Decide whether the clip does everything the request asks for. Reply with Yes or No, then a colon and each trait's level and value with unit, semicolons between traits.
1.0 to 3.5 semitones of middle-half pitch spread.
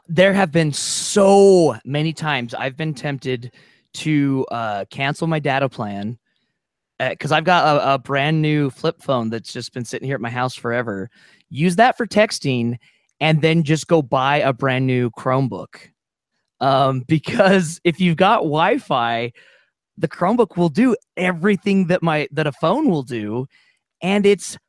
No: average, 5.1 semitones